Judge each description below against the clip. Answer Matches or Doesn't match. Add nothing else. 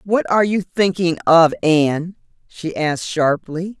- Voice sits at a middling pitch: Matches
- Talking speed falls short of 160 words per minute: Matches